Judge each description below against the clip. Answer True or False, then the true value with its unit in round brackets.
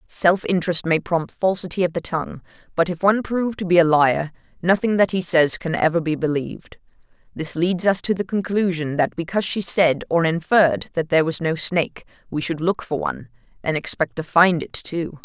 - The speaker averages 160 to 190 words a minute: False (200 wpm)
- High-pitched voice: False (170 Hz)